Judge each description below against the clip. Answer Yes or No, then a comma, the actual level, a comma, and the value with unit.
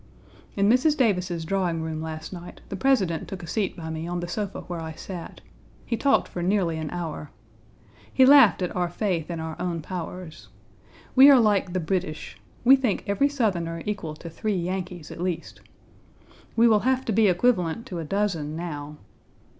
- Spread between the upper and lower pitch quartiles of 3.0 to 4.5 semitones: Yes, average, 4.2 semitones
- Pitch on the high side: No, medium, 180 Hz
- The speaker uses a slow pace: No, average, 185 wpm